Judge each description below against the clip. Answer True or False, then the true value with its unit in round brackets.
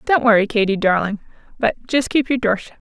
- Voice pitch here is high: True (225 Hz)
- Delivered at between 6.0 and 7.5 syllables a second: False (5.6 syllables/s)